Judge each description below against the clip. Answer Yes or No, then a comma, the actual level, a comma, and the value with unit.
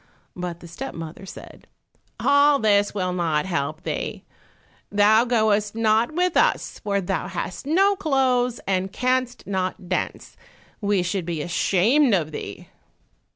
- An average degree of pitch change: No, wide, 5.7 semitones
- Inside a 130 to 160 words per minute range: Yes, average, 140 wpm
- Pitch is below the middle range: No, high, 205 Hz